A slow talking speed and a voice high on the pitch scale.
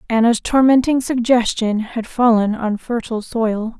Yes: slow, 125 wpm; high, 230 Hz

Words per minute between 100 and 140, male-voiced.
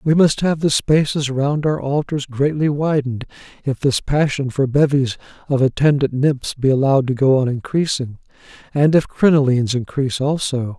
No: average, 155 wpm; male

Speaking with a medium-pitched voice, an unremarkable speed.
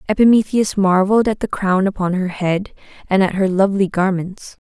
No: high, 195 Hz; average, 165 wpm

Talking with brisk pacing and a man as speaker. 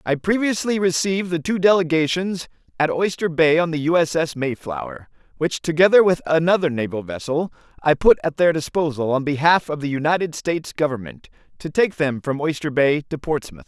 No: average, 180 wpm; male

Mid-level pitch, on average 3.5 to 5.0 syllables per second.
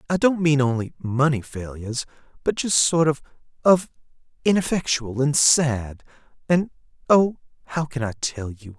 Yes: medium, 145 Hz; 4.6 syllables/s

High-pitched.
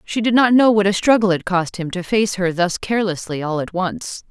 Yes: high, 195 Hz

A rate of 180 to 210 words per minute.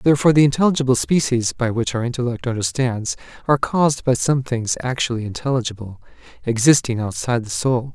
No: average, 150 wpm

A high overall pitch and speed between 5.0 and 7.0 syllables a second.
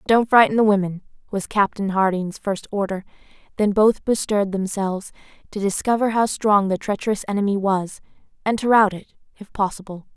Yes: high, 205 Hz; 5.5 syllables/s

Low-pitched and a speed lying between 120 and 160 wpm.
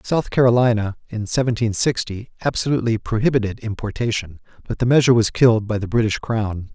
Yes: low, 115 Hz; average, 150 wpm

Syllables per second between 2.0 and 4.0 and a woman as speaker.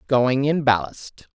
Yes: 3.6 syllables/s; female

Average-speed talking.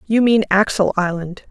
Yes: average, 160 wpm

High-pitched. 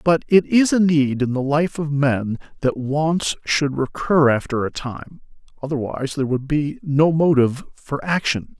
No: medium, 145 Hz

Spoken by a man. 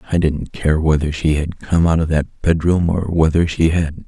Yes: male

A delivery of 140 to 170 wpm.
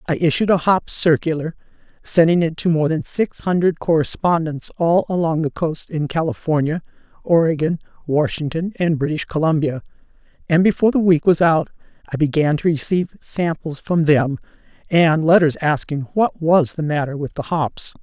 Yes: average, 155 wpm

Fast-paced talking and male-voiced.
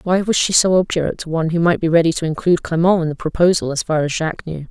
No: fast, 280 wpm; female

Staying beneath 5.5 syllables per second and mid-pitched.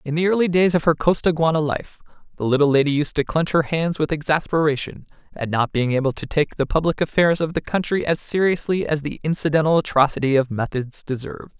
No: 5.9 syllables/s; medium, 155 Hz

